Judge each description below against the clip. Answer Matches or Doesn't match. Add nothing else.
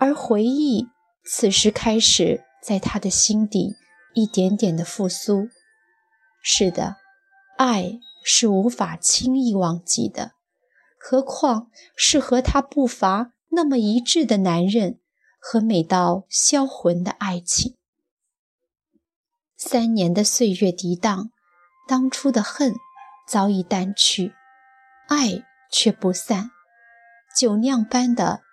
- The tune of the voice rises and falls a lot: Doesn't match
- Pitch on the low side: Doesn't match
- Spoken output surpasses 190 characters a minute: Doesn't match